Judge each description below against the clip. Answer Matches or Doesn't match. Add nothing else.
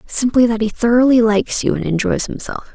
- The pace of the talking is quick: Doesn't match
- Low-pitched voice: Doesn't match